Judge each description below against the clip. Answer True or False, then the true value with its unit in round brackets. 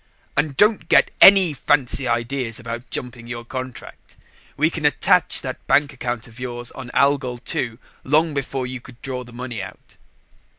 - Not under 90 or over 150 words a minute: False (165 wpm)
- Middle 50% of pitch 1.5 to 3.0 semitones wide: True (2.6 semitones)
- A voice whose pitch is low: True (125 Hz)